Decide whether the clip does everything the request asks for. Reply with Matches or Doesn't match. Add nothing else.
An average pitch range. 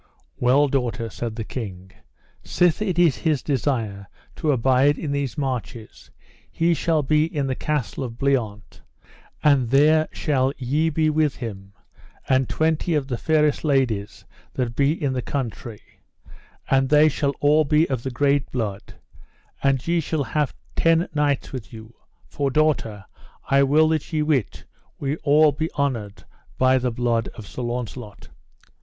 Matches